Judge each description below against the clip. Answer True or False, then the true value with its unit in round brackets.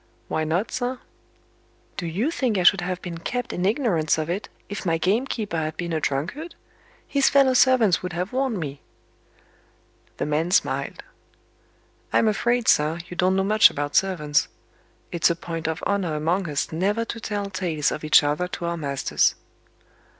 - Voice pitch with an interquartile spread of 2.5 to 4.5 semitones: False (5.2 semitones)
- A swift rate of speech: False (170 wpm)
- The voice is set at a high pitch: False (180 Hz)